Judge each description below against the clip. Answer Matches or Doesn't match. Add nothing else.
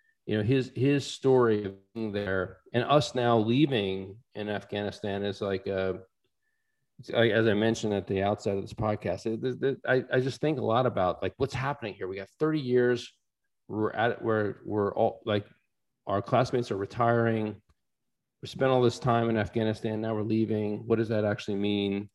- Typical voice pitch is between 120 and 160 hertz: Doesn't match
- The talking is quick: Doesn't match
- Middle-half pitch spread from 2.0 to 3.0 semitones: Doesn't match